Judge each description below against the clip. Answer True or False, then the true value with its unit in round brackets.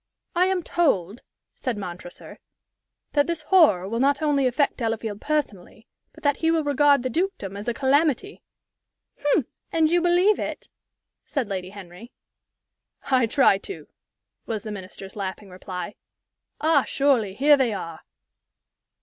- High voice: True (255 Hz)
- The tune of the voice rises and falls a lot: True (7.1 semitones)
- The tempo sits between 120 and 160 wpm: True (140 wpm)